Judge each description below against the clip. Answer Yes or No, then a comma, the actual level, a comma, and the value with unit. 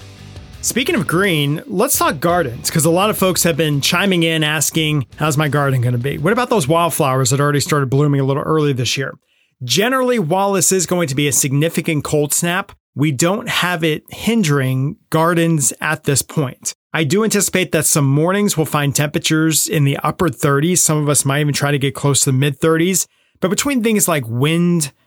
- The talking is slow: No, fast, 205 wpm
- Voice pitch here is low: No, medium, 155 Hz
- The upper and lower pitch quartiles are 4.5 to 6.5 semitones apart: No, average, 3.6 semitones